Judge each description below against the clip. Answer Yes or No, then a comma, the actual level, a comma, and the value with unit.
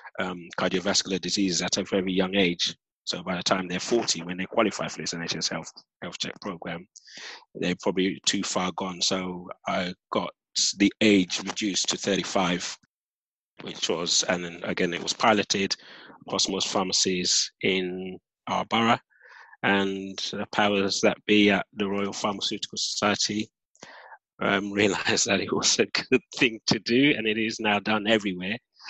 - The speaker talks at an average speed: Yes, average, 160 wpm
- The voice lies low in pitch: Yes, very low, 95 Hz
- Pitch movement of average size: No, narrow, 2.1 semitones